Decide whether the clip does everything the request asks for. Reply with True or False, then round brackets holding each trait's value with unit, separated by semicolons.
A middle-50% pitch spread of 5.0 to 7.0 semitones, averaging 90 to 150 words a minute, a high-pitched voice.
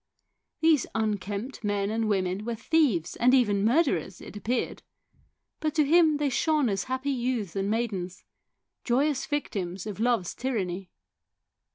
True (5.4 semitones; 140 wpm; 225 Hz)